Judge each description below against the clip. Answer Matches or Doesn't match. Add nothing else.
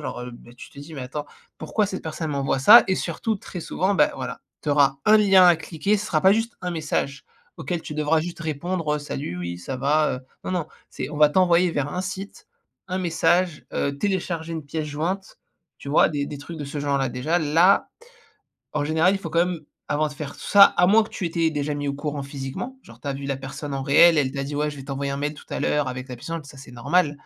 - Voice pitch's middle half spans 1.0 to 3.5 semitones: Doesn't match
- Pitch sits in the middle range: Matches